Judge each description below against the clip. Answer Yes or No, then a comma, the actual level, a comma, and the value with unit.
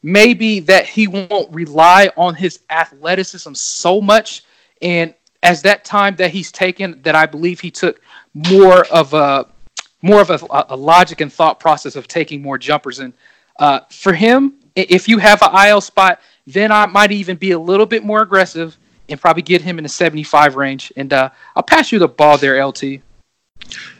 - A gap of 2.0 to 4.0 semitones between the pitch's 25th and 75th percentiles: No, average, 4.5 semitones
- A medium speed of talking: Yes, average, 185 wpm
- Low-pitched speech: No, medium, 175 Hz